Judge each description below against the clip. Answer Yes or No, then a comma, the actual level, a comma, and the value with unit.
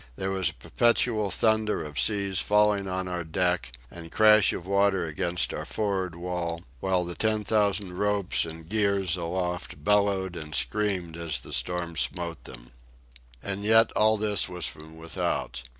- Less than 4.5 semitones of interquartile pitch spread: Yes, average, 3.3 semitones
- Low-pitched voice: Yes, very low, 95 Hz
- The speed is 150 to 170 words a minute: Yes, average, 160 wpm